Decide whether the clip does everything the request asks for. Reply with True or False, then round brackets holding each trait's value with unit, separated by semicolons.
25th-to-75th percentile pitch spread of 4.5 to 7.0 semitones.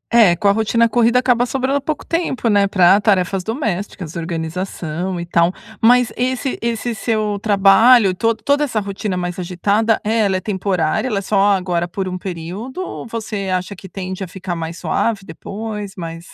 False (3.9 semitones)